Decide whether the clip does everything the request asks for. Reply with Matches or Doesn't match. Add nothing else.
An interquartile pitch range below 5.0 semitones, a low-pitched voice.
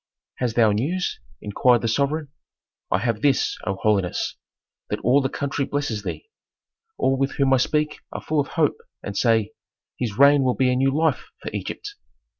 Matches